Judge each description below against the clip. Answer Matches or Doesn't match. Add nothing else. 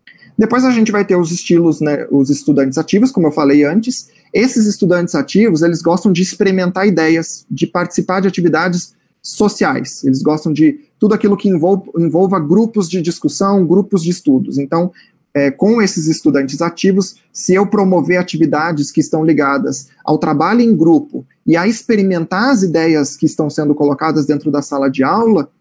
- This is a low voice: Doesn't match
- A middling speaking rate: Matches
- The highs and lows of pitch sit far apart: Doesn't match